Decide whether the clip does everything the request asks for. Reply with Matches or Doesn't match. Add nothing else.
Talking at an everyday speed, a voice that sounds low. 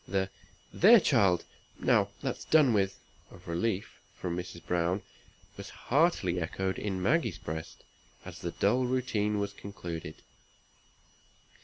Doesn't match